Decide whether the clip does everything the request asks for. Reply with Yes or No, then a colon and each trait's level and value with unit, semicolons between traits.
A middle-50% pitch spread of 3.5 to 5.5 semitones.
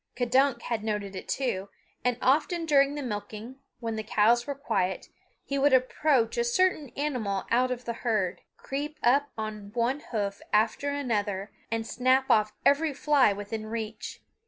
Yes: average, 4.4 semitones